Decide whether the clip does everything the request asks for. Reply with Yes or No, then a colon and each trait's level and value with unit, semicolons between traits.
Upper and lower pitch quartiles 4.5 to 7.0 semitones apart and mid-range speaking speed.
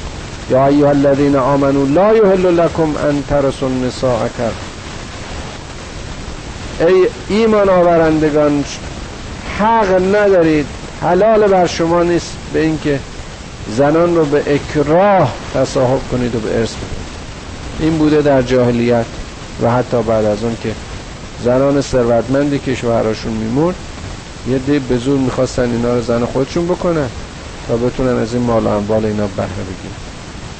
Yes: average, 5.2 semitones; average, 125 wpm